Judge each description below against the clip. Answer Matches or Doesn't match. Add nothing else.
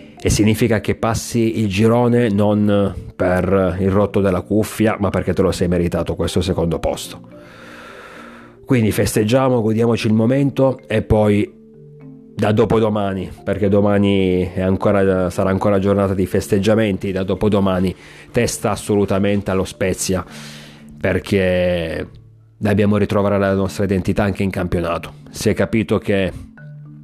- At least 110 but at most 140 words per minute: Matches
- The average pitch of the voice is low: Matches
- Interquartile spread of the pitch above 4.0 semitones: Doesn't match